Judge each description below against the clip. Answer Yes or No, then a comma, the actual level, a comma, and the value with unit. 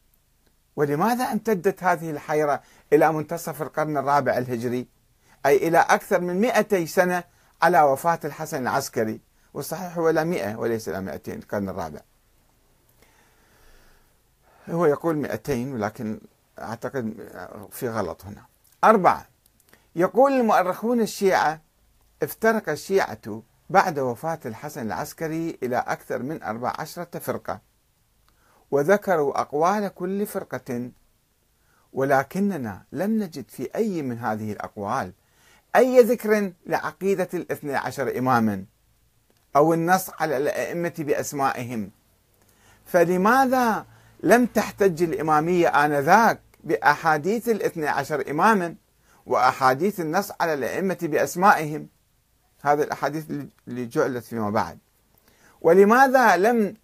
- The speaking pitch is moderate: Yes, medium, 155 Hz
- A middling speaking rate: Yes, average, 100 wpm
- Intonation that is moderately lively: No, wide, 7.3 semitones